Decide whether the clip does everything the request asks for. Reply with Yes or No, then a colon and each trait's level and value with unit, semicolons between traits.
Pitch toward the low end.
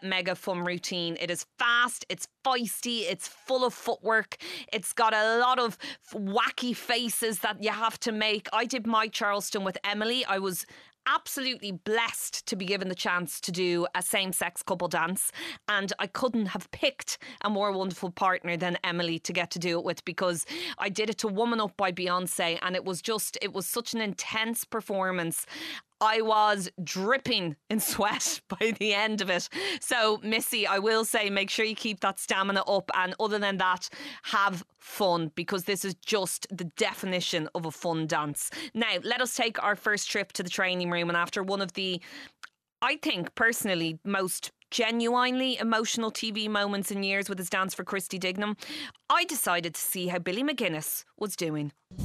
No: high, 200 Hz